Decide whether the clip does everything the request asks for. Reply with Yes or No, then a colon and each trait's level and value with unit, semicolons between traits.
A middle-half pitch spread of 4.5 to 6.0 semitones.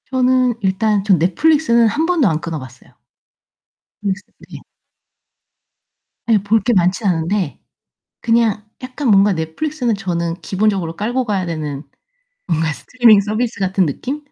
Yes: wide, 5.6 semitones